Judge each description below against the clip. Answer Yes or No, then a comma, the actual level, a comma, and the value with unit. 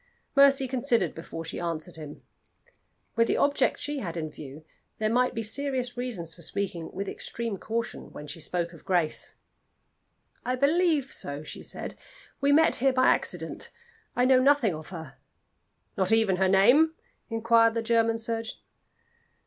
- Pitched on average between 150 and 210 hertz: No, high, 225 Hz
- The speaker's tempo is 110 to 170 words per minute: Yes, average, 155 wpm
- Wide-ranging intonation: Yes, wide, 6.9 semitones